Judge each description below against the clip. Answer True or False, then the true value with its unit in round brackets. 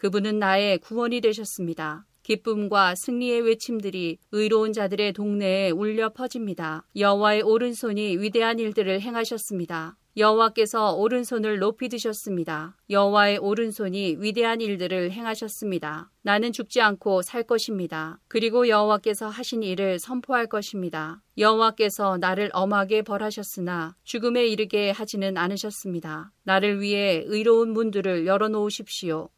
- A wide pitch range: False (2.8 semitones)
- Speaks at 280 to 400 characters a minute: True (350 characters per minute)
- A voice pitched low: False (210 Hz)